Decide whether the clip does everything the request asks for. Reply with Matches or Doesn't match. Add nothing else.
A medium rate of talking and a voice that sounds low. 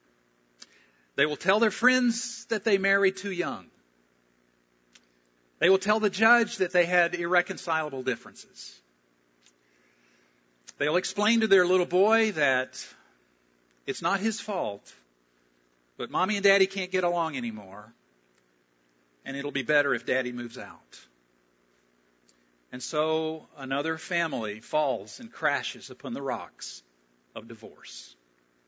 Doesn't match